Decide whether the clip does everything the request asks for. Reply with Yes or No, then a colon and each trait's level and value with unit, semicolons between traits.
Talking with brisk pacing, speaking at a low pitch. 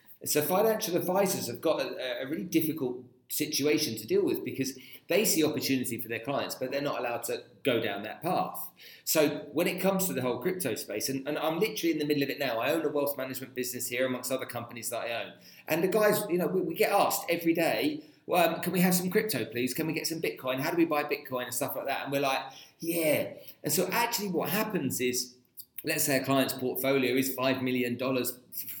No: fast, 235 wpm; medium, 145 Hz